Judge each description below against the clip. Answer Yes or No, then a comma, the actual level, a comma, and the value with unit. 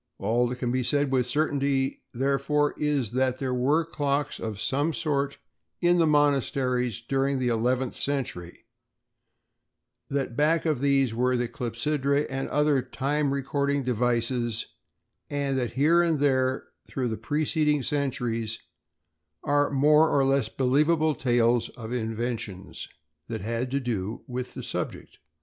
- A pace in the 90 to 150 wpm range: Yes, average, 140 wpm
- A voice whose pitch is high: No, low, 135 Hz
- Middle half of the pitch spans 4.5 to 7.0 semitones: No, average, 2.9 semitones